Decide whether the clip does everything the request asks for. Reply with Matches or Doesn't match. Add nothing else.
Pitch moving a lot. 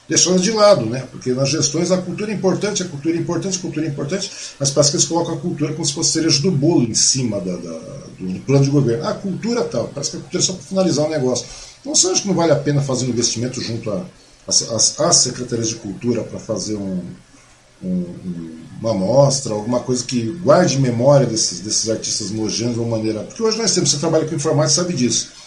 Matches